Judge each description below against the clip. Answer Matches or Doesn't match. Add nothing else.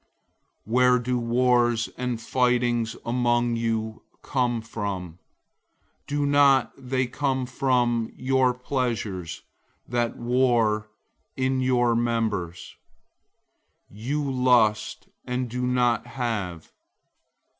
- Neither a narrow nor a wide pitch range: Doesn't match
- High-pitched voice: Doesn't match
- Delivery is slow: Matches